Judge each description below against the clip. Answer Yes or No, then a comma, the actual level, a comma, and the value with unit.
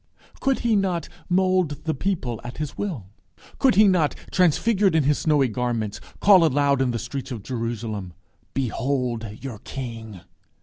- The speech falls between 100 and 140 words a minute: No, average, 155 wpm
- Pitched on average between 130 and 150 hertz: Yes, medium, 140 Hz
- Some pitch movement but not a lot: No, wide, 7.2 semitones